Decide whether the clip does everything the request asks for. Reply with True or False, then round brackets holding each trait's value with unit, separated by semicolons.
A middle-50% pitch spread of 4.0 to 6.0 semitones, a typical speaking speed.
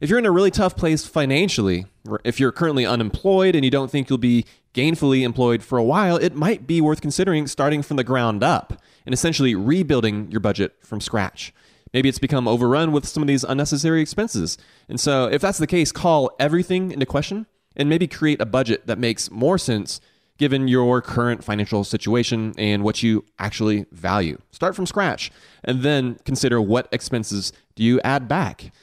True (5.6 semitones; 190 wpm)